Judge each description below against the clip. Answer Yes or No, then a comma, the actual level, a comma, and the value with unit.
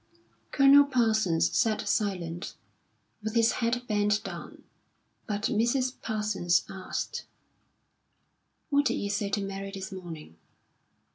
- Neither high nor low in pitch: No, high, 210 Hz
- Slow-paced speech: Yes, slow, 115 wpm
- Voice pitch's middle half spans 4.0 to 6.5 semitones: No, average, 3.1 semitones